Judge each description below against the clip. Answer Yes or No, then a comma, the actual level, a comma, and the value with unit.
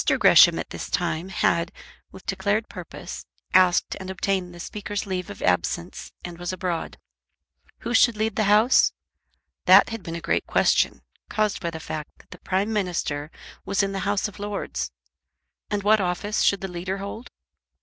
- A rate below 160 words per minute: No, average, 170 wpm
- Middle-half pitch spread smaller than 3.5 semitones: Yes, average, 3.0 semitones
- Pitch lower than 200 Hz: Yes, high, 190 Hz